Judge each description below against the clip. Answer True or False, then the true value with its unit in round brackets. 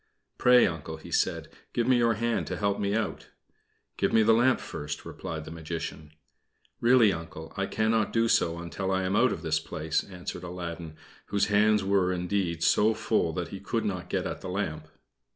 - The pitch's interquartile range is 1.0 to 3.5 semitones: False (4.9 semitones)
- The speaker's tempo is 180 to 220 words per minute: True (190 wpm)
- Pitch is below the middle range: True (95 Hz)